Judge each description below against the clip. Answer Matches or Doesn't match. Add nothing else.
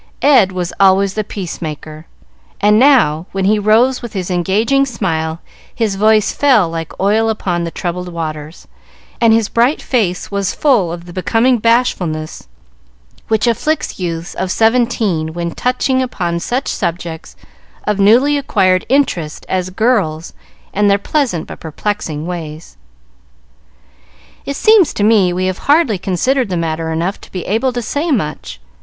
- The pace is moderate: Matches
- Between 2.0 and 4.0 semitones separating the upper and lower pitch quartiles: Doesn't match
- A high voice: Matches